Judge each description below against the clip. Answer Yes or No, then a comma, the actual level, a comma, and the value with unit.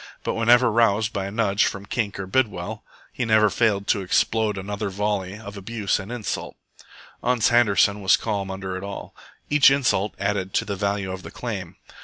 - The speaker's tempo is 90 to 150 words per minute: No, average, 185 wpm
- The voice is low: Yes, low, 105 Hz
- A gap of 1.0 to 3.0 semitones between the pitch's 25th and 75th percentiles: Yes, narrow, 2.5 semitones